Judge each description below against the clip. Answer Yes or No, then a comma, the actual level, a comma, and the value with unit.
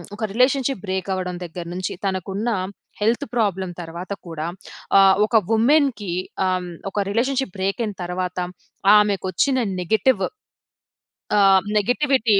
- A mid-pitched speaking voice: No, high, 200 Hz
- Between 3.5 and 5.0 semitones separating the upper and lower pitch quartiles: Yes, average, 4.2 semitones